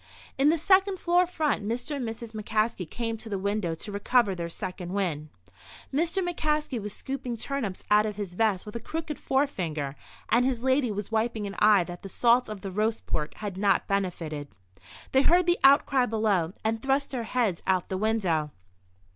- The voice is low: No, high, 220 Hz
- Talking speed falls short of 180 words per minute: No, average, 190 wpm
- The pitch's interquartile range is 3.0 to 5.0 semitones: No, wide, 5.6 semitones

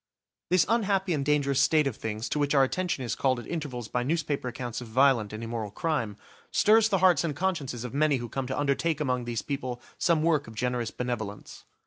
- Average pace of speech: No, fast, 210 wpm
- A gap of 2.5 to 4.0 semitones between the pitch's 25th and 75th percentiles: No, average, 4.5 semitones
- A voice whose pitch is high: No, low, 135 Hz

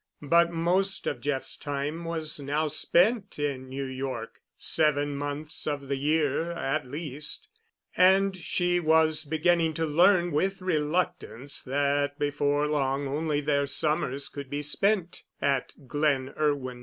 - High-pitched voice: No, medium, 150 Hz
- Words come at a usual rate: No, slow, 130 wpm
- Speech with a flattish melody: No, average, 3.1 semitones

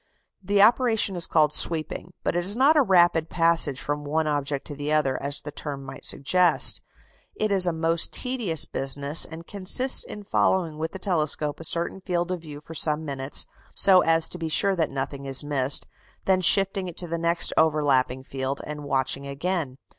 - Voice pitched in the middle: Yes, medium, 160 Hz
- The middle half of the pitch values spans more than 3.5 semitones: Yes, average, 4.1 semitones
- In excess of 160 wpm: Yes, average, 190 wpm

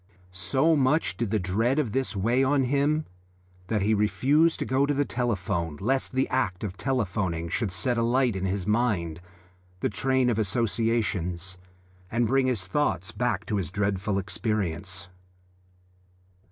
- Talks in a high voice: No, low, 110 Hz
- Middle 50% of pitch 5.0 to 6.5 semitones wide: Yes, wide, 5.5 semitones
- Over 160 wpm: No, average, 155 wpm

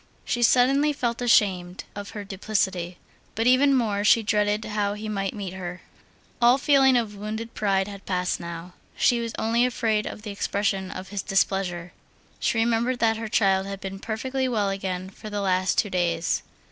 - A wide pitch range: No, average, 3.2 semitones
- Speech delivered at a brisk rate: No, average, 180 wpm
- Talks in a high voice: Yes, high, 205 Hz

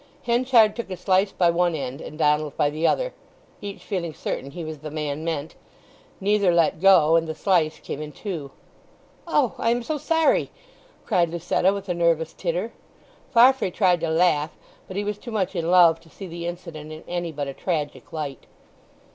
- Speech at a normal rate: Yes, average, 190 wpm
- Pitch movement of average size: Yes, average, 4.2 semitones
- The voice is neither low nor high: Yes, medium, 170 Hz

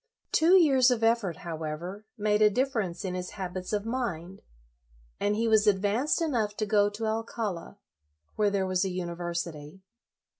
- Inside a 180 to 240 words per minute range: No, average, 155 wpm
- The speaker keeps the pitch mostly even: No, average, 3.7 semitones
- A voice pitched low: No, high, 205 Hz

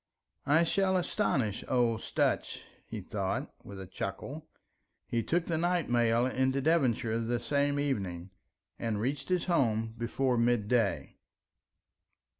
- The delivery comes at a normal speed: No, slow, 125 wpm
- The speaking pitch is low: Yes, low, 125 Hz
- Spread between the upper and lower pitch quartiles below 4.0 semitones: No, average, 4.6 semitones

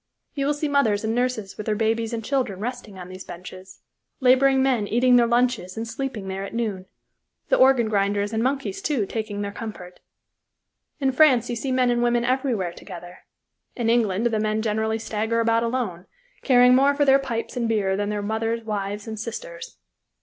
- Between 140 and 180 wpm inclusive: No, average, 190 wpm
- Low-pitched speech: No, high, 230 Hz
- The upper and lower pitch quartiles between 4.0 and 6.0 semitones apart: No, average, 3.6 semitones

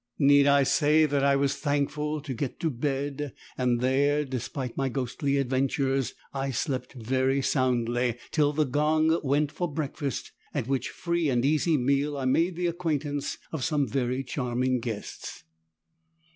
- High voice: No, medium, 140 Hz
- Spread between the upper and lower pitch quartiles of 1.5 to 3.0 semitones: Yes, narrow, 2.4 semitones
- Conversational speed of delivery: Yes, average, 155 wpm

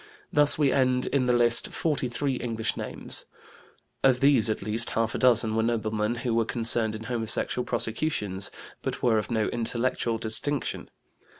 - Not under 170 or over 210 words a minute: No, average, 160 wpm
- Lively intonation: No, narrow, 2.4 semitones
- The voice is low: Yes, low, 115 Hz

